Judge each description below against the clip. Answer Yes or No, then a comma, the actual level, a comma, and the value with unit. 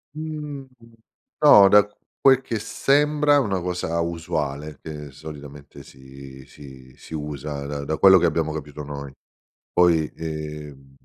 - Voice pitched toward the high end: No, very low, 75 Hz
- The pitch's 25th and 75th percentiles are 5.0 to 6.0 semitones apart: Yes, wide, 5.4 semitones